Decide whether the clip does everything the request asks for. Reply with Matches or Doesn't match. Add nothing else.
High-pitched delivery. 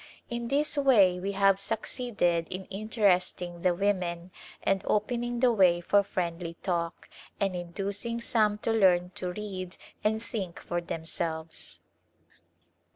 Matches